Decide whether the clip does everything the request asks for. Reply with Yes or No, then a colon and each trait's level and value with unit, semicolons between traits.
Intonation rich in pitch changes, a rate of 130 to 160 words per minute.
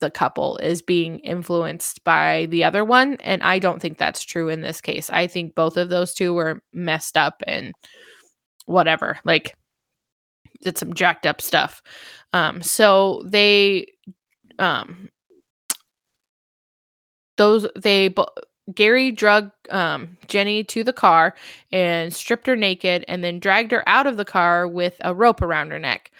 No: average, 3.5 semitones; average, 150 wpm